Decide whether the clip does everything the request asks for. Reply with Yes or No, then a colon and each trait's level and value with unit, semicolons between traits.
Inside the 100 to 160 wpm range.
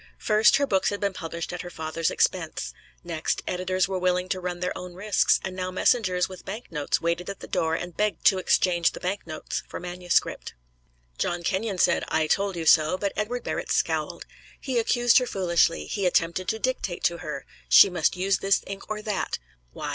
No: average, 200 wpm